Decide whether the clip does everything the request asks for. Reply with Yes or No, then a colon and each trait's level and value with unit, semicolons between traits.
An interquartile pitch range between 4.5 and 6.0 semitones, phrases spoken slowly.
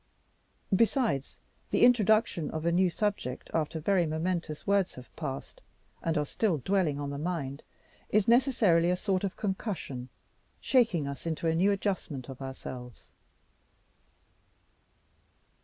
Yes: wide, 5.6 semitones; slow, 130 wpm